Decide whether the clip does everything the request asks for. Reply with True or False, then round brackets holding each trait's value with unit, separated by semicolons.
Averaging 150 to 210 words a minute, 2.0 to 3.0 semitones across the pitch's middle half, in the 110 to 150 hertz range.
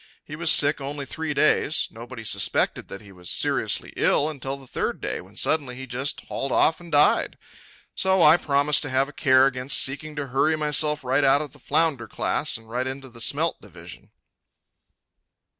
True (190 wpm; 2.5 semitones; 140 Hz)